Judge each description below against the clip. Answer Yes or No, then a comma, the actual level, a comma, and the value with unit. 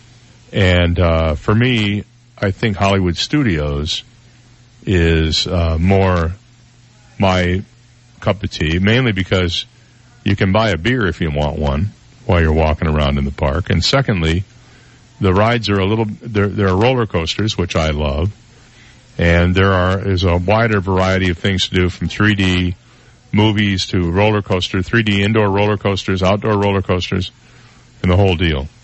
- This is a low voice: Yes, low, 100 Hz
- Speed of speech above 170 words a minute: No, average, 155 wpm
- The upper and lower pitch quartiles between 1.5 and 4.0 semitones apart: No, average, 4.7 semitones